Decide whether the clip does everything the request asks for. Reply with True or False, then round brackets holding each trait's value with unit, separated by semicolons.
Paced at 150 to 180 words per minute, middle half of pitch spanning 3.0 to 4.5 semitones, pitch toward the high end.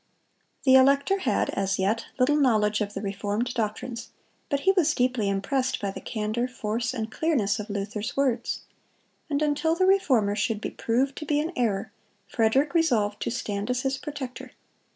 False (170 wpm; 5.0 semitones; 245 Hz)